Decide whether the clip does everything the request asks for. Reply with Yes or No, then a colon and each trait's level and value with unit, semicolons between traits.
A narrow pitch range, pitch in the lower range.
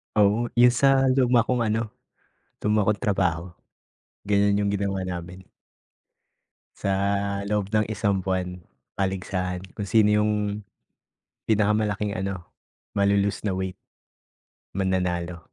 Yes: narrow, 2.1 semitones; low, 100 Hz